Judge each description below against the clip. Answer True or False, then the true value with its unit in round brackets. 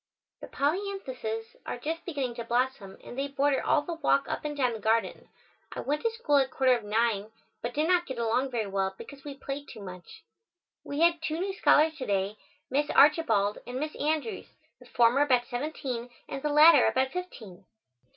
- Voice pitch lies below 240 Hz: False (270 Hz)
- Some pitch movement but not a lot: True (4.6 semitones)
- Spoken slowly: False (195 wpm)